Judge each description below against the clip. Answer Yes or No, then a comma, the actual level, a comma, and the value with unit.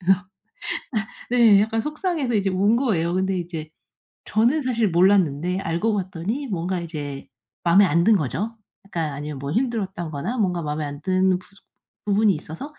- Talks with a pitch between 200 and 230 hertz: No, medium, 185 Hz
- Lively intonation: No, average, 5.0 semitones